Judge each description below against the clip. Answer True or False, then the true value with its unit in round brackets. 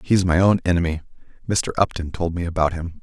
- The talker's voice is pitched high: False (85 Hz)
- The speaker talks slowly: False (200 wpm)